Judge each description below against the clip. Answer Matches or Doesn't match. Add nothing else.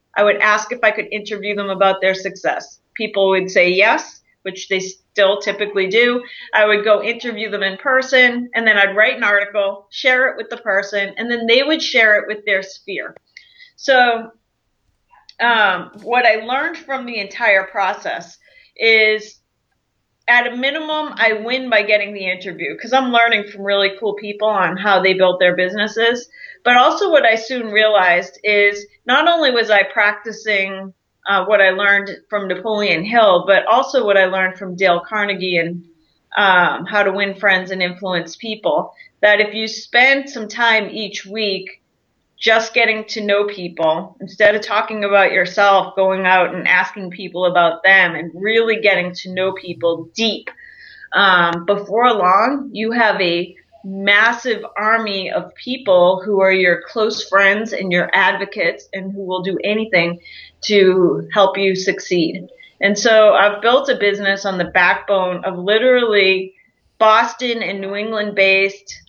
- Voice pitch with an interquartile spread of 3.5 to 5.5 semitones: Doesn't match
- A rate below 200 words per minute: Matches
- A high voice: Matches